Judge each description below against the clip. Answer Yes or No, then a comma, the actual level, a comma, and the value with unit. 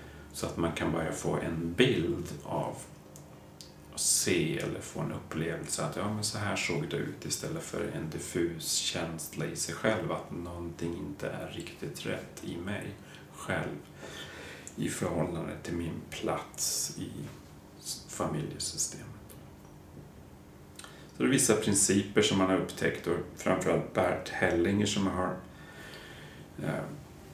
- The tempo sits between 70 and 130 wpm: No, average, 140 wpm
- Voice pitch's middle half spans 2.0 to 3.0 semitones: No, average, 3.9 semitones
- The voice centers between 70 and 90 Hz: Yes, very low, 85 Hz